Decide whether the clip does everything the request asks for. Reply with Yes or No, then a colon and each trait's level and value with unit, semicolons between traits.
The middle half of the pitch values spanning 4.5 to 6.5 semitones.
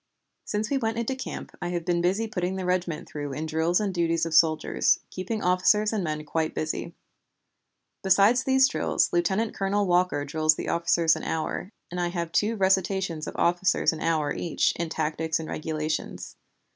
No: average, 3.4 semitones